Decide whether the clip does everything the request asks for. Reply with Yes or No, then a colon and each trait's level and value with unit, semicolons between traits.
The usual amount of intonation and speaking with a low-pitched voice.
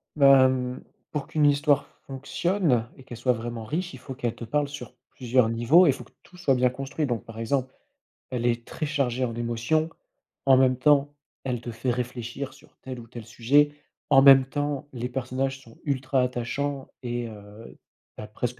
Yes: average, 3.0 semitones; low, 130 Hz